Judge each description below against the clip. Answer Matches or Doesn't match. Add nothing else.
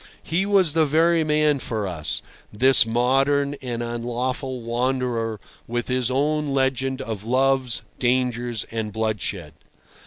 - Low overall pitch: Matches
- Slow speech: Matches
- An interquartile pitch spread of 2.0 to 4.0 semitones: Matches